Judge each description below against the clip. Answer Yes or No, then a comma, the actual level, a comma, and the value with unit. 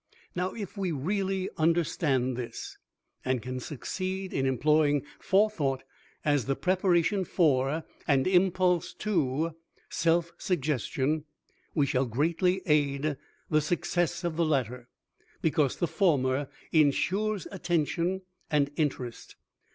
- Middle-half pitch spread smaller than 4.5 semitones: No, average, 4.8 semitones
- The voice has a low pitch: No, medium, 155 Hz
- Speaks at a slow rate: Yes, slow, 110 wpm